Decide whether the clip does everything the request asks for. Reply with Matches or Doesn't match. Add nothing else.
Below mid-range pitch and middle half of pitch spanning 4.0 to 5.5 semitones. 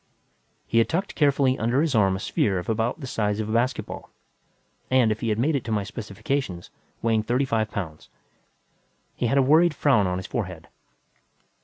Matches